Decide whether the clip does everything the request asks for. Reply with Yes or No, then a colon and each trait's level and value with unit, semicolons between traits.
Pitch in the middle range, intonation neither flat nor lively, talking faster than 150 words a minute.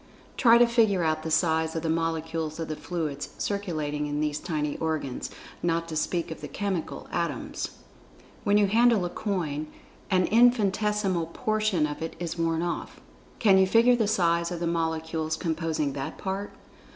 Yes: medium, 170 Hz; average, 3.9 semitones; average, 170 wpm